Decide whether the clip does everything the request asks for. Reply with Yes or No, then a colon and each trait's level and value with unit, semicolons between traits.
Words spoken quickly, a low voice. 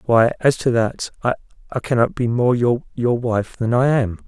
No: average, 170 wpm; low, 120 Hz